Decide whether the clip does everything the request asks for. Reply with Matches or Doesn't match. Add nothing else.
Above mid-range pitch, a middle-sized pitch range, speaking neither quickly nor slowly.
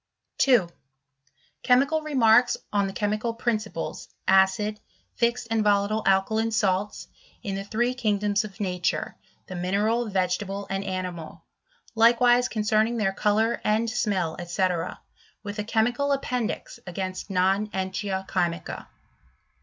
Doesn't match